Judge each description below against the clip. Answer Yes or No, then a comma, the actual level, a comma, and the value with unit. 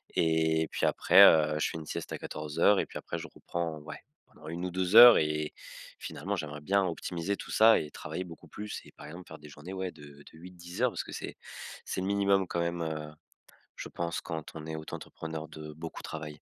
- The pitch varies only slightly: No, average, 3.1 semitones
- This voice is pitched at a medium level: No, very low, 80 Hz